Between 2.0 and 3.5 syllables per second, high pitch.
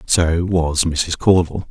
No: 3.1 syllables/s; very low, 85 Hz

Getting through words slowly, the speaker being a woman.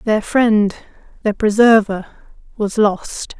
Yes: slow, 105 wpm; female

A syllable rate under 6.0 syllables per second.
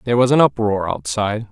No: 6.5 syllables/s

